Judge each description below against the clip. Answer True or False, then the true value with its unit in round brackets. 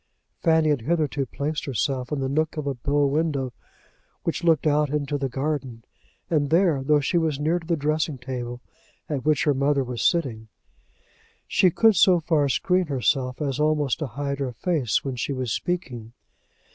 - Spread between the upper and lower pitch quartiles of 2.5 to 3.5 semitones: True (3.0 semitones)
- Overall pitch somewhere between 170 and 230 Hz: False (145 Hz)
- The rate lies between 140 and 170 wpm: False (180 wpm)